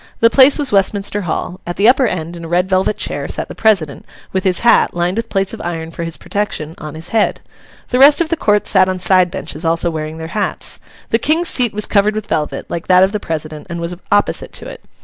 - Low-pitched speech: No, medium, 185 Hz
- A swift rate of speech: Yes, fast, 245 wpm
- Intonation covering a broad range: No, average, 4.3 semitones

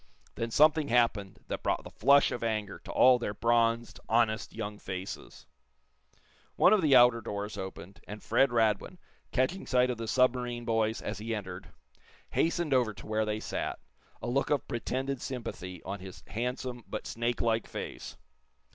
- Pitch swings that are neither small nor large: Yes, average, 3.0 semitones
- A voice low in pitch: Yes, low, 115 Hz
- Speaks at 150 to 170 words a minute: Yes, average, 165 wpm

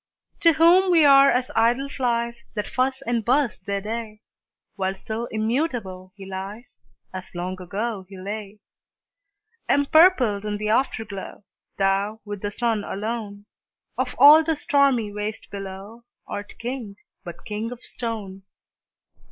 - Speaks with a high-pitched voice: Yes, high, 220 Hz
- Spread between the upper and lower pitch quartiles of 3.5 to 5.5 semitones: Yes, average, 4.0 semitones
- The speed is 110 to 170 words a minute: Yes, slow, 135 wpm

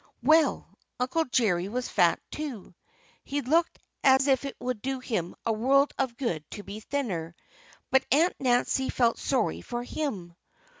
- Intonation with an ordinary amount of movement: Yes, average, 4.3 semitones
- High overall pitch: Yes, very high, 250 Hz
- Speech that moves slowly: No, average, 155 wpm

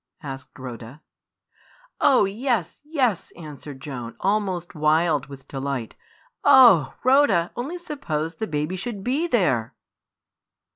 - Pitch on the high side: No, medium, 170 Hz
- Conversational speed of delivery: No, slow, 110 wpm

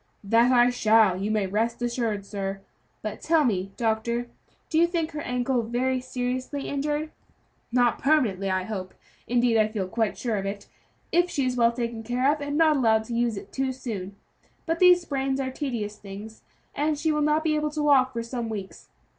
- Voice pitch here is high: Yes, high, 240 Hz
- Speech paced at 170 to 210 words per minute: Yes, average, 195 wpm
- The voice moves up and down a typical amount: Yes, average, 4.6 semitones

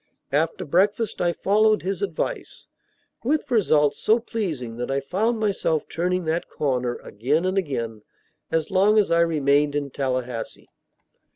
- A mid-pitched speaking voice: Yes, medium, 165 Hz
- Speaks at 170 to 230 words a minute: No, average, 145 wpm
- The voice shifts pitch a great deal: Yes, wide, 6.2 semitones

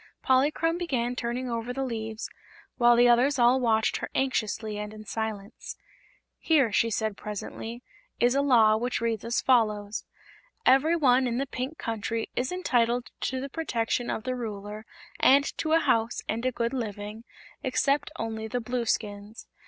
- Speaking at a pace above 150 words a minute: Yes, average, 160 wpm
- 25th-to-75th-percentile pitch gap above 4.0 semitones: No, average, 2.8 semitones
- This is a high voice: Yes, high, 235 Hz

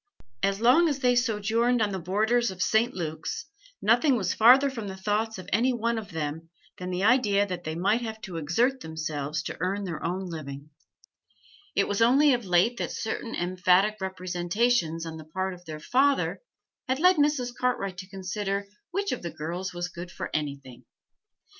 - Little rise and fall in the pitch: No, wide, 5.5 semitones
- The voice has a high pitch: Yes, high, 195 Hz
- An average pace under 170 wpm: No, average, 185 wpm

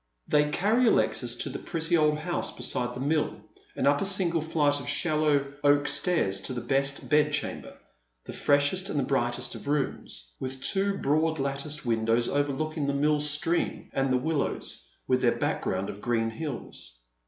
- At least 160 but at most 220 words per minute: Yes, average, 170 wpm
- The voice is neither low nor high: Yes, medium, 145 Hz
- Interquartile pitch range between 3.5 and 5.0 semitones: No, average, 3.0 semitones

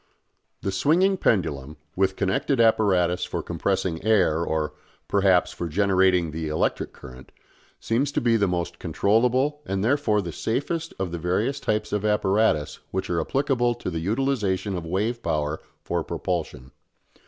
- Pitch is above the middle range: No, very low, 95 Hz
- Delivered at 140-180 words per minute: Yes, average, 150 wpm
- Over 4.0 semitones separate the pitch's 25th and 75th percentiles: Yes, average, 5.1 semitones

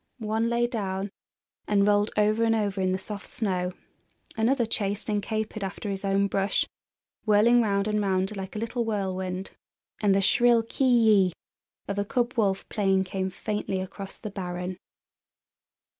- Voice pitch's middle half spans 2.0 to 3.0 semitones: Yes, narrow, 2.5 semitones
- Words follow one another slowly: No, average, 160 wpm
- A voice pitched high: Yes, high, 205 Hz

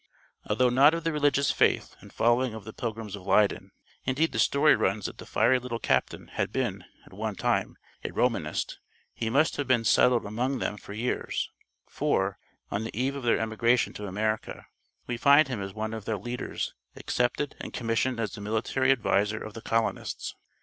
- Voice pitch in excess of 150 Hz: No, low, 115 Hz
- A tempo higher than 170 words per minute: Yes, average, 190 wpm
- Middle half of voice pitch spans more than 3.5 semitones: No, average, 3.2 semitones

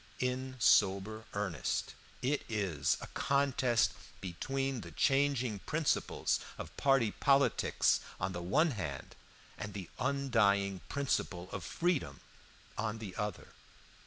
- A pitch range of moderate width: No, wide, 5.7 semitones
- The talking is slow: Yes, slow, 115 wpm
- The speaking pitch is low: Yes, low, 115 Hz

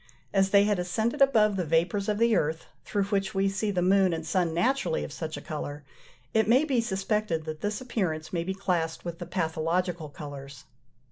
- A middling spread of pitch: Yes, average, 4.3 semitones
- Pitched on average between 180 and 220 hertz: Yes, medium, 185 Hz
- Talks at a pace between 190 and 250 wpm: Yes, average, 200 wpm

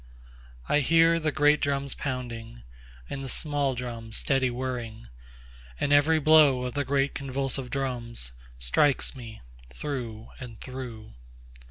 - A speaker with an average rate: No, slow, 115 wpm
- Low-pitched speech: Yes, low, 125 Hz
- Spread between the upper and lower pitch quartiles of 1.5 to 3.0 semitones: No, average, 4.4 semitones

